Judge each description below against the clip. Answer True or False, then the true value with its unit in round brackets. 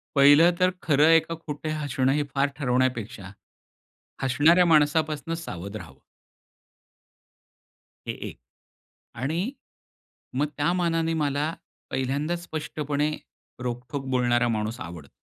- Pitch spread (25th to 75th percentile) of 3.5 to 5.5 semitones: True (4.3 semitones)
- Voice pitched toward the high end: False (145 Hz)